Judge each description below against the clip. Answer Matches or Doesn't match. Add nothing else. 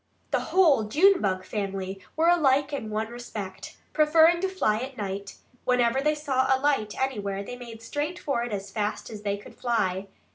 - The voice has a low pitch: Doesn't match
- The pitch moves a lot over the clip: Matches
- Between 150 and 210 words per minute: Matches